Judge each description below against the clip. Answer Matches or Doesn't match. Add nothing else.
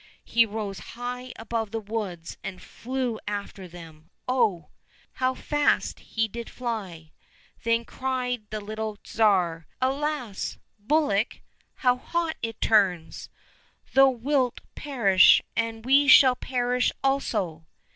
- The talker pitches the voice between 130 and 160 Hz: Doesn't match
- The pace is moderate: Doesn't match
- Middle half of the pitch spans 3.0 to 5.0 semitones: Matches